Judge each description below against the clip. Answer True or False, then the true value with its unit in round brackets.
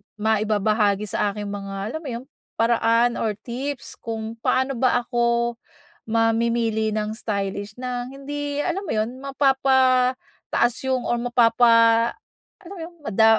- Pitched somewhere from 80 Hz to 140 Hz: False (235 Hz)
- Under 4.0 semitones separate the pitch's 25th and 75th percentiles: True (2.9 semitones)